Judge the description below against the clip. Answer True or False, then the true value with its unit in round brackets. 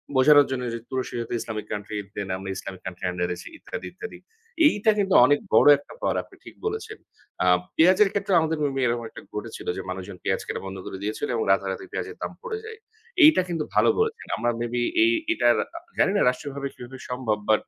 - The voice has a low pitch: True (130 Hz)